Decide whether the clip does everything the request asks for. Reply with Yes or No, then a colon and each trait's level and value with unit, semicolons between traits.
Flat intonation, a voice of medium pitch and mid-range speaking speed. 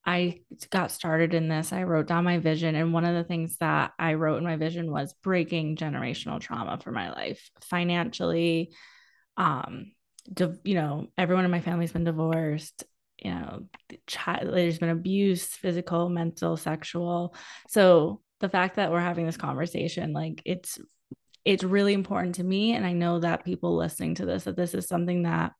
Yes: narrow, 1.7 semitones; medium, 170 Hz; average, 185 wpm